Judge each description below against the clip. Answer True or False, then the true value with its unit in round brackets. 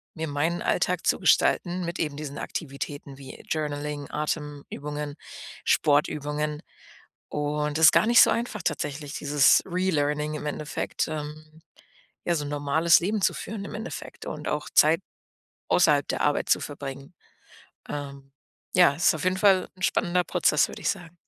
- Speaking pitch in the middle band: True (150 Hz)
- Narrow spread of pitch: False (3.0 semitones)